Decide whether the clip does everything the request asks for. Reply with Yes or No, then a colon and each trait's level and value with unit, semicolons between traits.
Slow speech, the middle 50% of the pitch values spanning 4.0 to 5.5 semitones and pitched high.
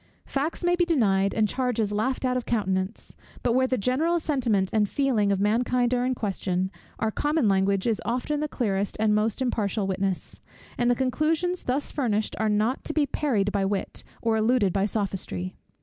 No: average, 185 wpm; average, 4.5 semitones; high, 225 Hz